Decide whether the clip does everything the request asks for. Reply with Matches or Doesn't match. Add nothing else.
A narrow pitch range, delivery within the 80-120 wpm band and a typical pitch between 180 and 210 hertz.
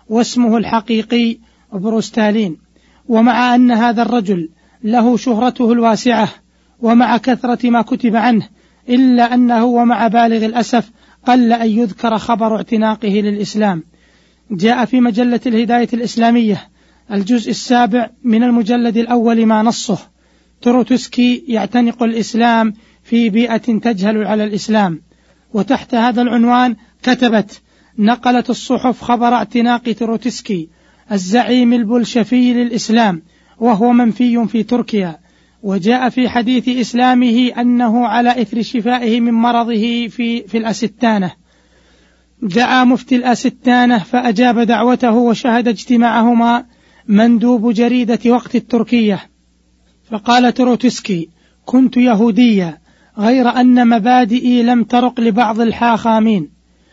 Doesn't match